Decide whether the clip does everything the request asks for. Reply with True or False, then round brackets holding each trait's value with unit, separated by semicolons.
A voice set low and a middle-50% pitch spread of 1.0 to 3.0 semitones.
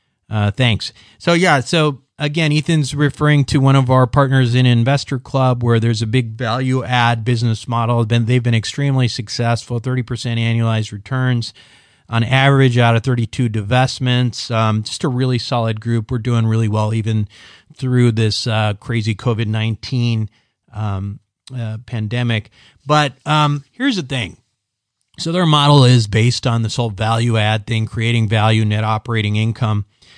True (120 Hz; 2.7 semitones)